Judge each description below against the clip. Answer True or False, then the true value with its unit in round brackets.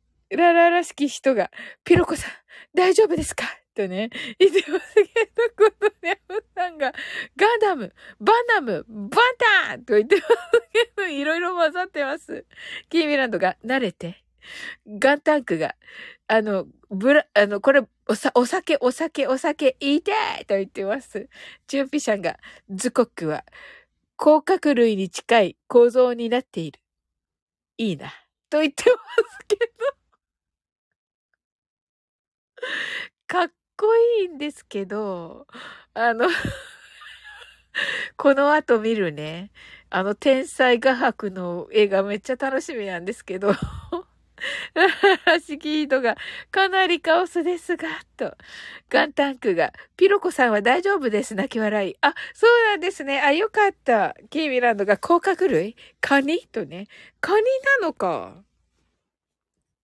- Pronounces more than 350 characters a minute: False (245 characters per minute)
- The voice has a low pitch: False (290 Hz)